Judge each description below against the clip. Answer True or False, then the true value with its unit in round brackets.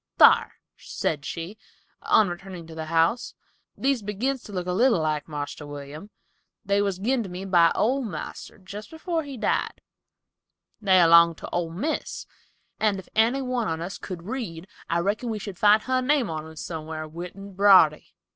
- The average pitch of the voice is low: False (190 Hz)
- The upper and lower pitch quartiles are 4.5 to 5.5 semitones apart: True (5.1 semitones)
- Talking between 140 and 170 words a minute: False (180 wpm)